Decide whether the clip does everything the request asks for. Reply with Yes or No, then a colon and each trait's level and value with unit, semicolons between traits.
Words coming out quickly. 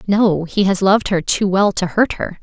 Yes: fast, 245 wpm